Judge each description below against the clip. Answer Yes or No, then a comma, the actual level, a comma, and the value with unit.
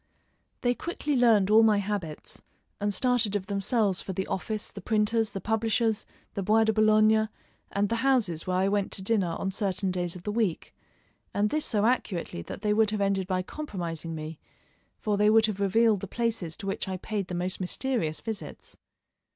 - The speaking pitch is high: Yes, high, 205 Hz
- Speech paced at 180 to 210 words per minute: Yes, average, 190 wpm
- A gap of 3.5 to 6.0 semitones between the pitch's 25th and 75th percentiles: No, average, 2.9 semitones